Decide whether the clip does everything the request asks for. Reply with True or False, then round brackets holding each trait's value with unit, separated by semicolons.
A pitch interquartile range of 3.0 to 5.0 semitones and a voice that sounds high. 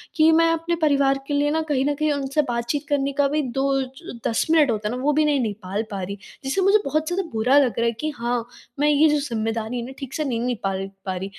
True (4.3 semitones; 270 Hz)